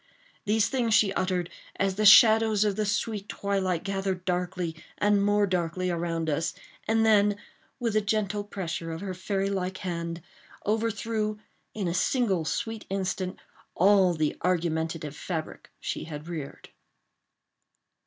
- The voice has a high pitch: Yes, high, 195 Hz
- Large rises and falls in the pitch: No, average, 3.3 semitones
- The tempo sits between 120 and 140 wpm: Yes, slow, 135 wpm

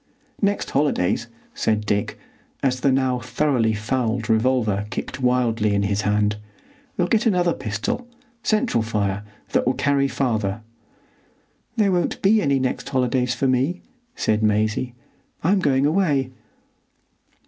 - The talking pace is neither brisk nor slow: No, slow, 125 wpm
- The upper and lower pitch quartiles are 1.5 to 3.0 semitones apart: No, average, 5.2 semitones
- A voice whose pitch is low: Yes, low, 125 Hz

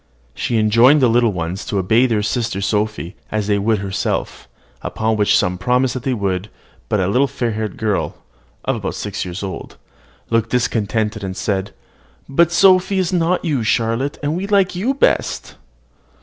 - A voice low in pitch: Yes, low, 115 Hz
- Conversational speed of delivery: Yes, average, 175 wpm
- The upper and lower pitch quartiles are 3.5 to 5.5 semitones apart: Yes, average, 4.6 semitones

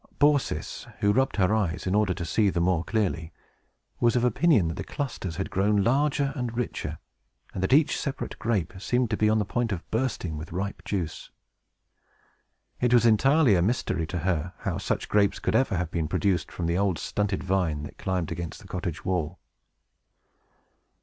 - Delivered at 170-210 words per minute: Yes, average, 185 wpm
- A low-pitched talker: Yes, low, 100 Hz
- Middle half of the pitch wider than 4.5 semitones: Yes, average, 5.2 semitones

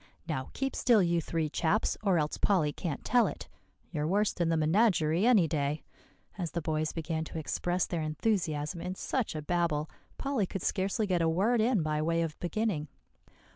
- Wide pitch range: No, average, 4.3 semitones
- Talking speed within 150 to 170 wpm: No, average, 185 wpm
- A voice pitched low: No, medium, 170 Hz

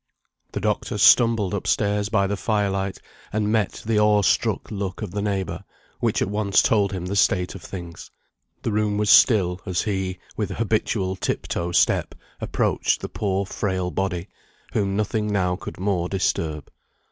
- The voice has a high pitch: No, low, 100 Hz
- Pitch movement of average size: No, narrow, 2.1 semitones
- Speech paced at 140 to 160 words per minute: No, average, 170 wpm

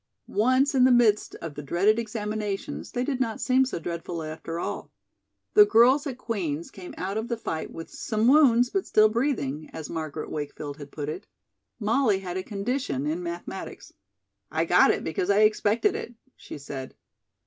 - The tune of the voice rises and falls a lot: Yes, wide, 6.8 semitones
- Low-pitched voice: No, high, 205 Hz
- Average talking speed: Yes, average, 180 wpm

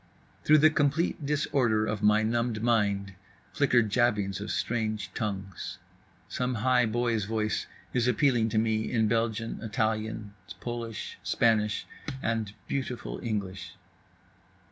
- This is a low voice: Yes, low, 110 Hz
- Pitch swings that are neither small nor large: No, narrow, 2.2 semitones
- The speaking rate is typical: No, slow, 115 wpm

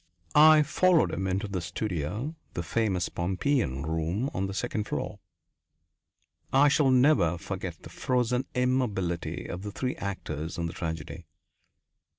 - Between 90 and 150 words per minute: Yes, average, 140 wpm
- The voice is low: Yes, low, 100 Hz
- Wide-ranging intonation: Yes, wide, 7.0 semitones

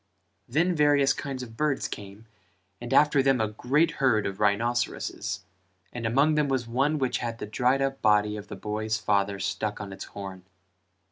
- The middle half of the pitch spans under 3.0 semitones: No, average, 4.5 semitones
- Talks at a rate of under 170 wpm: No, average, 180 wpm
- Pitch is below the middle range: Yes, low, 120 Hz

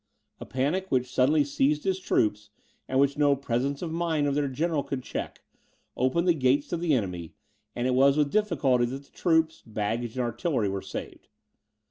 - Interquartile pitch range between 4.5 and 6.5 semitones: No, average, 4.0 semitones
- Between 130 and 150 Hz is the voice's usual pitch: Yes, medium, 140 Hz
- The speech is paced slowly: No, average, 185 wpm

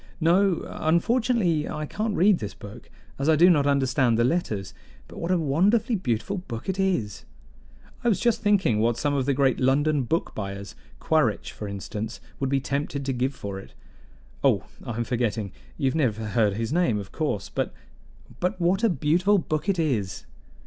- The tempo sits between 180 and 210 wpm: Yes, average, 185 wpm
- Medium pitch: Yes, medium, 145 Hz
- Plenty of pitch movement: Yes, wide, 7.5 semitones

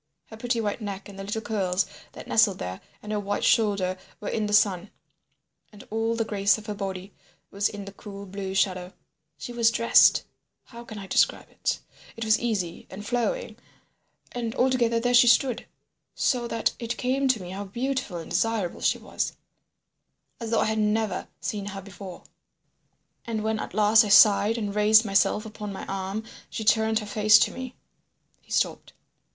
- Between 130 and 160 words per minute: No, average, 180 wpm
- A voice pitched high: Yes, high, 210 Hz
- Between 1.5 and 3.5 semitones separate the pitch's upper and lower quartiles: Yes, narrow, 2.5 semitones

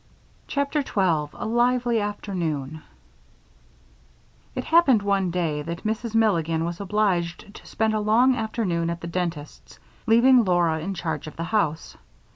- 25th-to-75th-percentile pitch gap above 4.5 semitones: Yes, average, 5.1 semitones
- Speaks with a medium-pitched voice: No, high, 195 Hz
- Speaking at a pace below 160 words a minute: Yes, average, 140 wpm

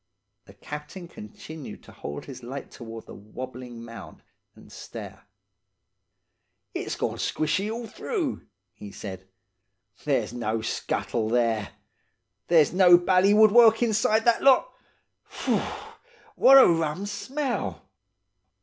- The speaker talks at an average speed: No, slow, 115 wpm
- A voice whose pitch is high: No, medium, 155 Hz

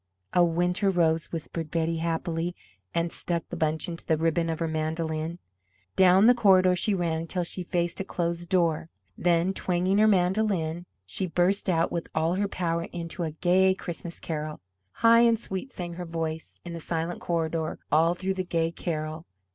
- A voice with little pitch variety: Yes, narrow, 2.0 semitones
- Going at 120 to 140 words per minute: No, average, 180 wpm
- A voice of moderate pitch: Yes, medium, 170 Hz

